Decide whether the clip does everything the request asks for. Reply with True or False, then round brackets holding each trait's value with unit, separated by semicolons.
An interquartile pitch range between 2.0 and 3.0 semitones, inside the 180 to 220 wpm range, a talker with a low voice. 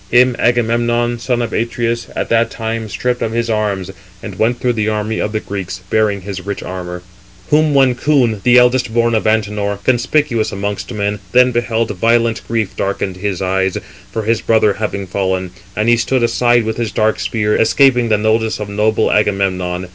True (2.7 semitones; 185 wpm; 110 Hz)